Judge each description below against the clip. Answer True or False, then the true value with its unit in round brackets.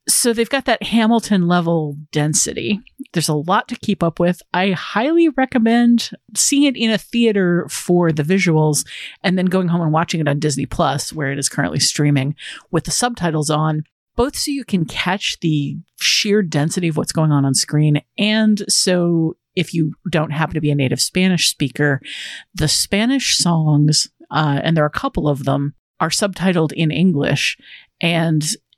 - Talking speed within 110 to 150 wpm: False (180 wpm)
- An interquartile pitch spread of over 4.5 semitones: True (5.3 semitones)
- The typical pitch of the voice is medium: True (170 Hz)